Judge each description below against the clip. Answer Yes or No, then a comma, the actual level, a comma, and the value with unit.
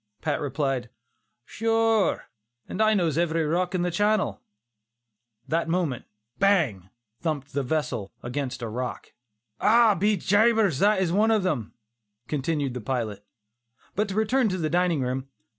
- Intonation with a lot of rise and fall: Yes, wide, 7.4 semitones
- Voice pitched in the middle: Yes, medium, 165 Hz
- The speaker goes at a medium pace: Yes, average, 150 wpm